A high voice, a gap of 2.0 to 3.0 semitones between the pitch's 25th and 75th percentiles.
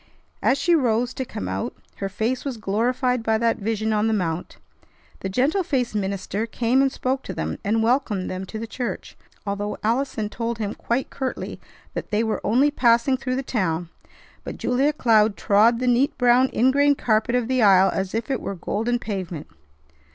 No: high, 230 Hz; average, 3.6 semitones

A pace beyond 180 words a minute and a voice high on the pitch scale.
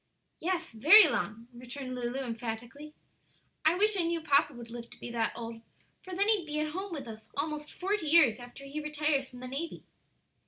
Yes: average, 195 wpm; very high, 285 Hz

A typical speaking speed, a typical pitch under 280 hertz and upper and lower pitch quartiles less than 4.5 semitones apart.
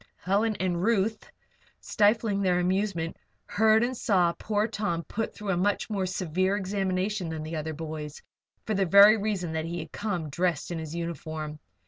Yes: average, 170 wpm; medium, 185 Hz; average, 3.9 semitones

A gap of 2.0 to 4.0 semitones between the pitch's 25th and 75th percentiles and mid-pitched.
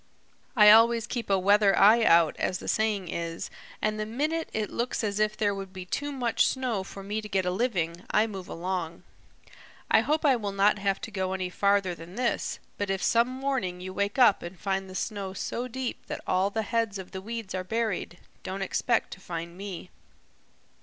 No: average, 3.4 semitones; high, 200 Hz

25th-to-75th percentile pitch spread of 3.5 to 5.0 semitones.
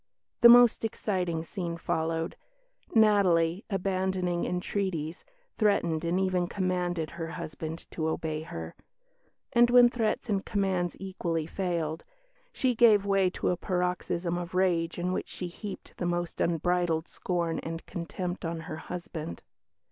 No: average, 2.7 semitones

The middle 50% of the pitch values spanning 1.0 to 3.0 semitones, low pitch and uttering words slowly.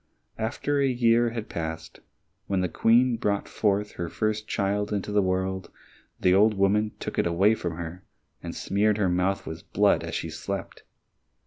No: average, 2.7 semitones; low, 100 Hz; average, 170 wpm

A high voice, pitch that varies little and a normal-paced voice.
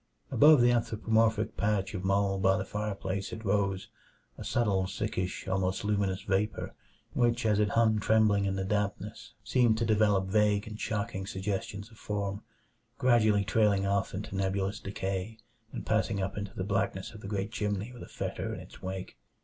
No: low, 100 Hz; narrow, 2.1 semitones; average, 175 wpm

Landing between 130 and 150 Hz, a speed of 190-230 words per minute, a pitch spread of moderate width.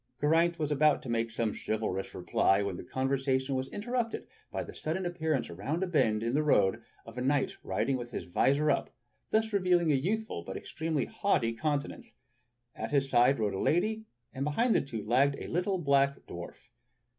No: medium, 140 Hz; average, 195 wpm; wide, 6.5 semitones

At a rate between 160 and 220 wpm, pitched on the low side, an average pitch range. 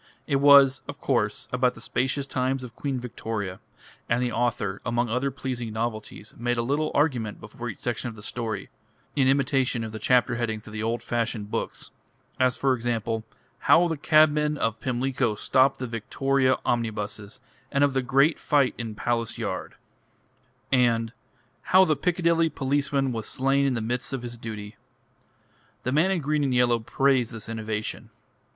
Yes: average, 170 wpm; low, 125 Hz; average, 3.3 semitones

